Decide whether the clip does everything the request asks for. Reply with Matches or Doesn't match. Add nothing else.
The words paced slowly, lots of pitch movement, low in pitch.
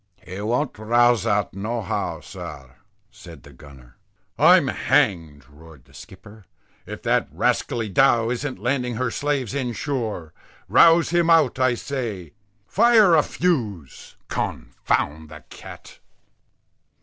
Matches